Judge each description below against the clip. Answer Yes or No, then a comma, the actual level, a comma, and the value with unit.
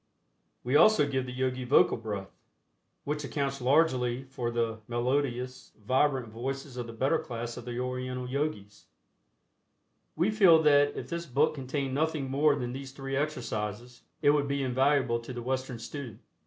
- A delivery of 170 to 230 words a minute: No, average, 160 wpm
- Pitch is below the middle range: Yes, low, 130 Hz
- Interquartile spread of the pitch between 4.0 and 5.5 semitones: No, average, 2.7 semitones